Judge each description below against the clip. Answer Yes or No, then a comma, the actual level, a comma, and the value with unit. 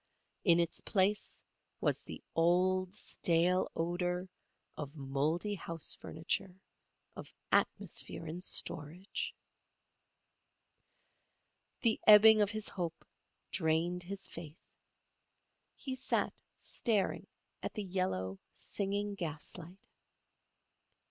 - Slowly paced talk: Yes, slow, 90 wpm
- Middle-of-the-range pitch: Yes, medium, 180 Hz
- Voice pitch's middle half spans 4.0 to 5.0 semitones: No, average, 3.3 semitones